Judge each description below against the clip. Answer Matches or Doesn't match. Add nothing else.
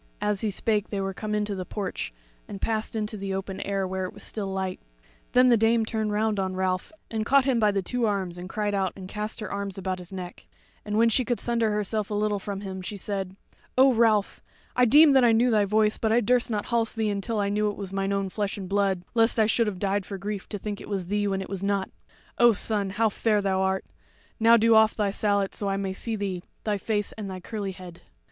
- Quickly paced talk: Matches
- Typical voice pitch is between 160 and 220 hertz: Matches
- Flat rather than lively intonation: Matches